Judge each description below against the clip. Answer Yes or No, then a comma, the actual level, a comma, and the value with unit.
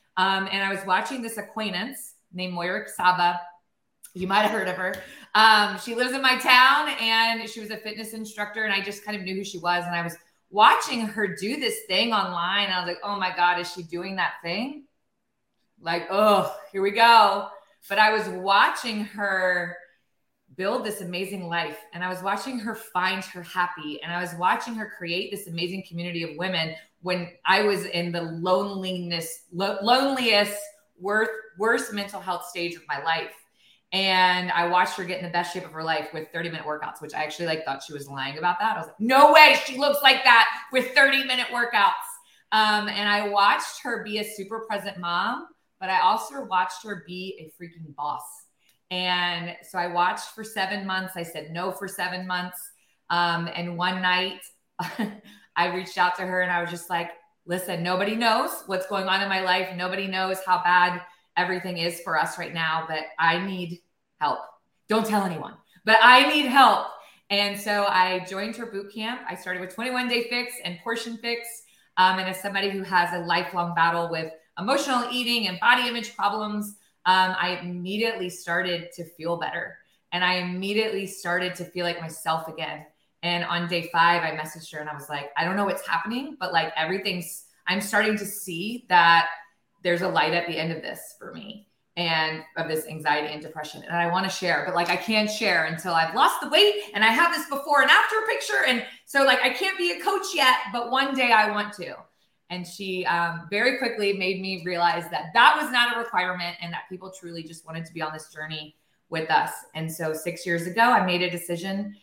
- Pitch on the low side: No, medium, 185 Hz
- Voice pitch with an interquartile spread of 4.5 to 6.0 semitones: No, average, 3.8 semitones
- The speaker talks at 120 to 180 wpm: No, fast, 205 wpm